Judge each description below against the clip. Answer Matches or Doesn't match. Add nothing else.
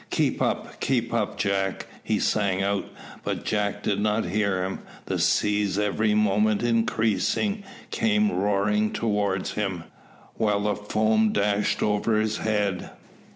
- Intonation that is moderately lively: Doesn't match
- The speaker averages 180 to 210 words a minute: Doesn't match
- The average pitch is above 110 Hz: Doesn't match